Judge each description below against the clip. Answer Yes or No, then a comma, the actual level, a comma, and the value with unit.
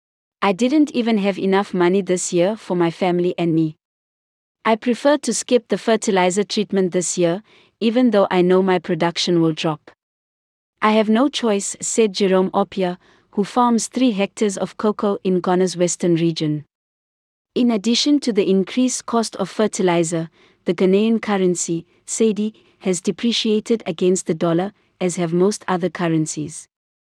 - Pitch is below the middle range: No, high, 190 Hz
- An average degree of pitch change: Yes, average, 3.9 semitones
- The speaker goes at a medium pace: Yes, average, 155 wpm